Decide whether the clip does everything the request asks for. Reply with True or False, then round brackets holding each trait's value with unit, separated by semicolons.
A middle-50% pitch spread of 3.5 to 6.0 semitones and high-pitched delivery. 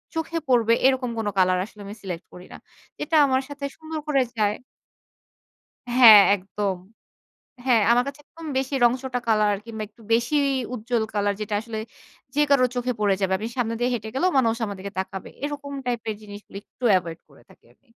True (4.2 semitones; 230 Hz)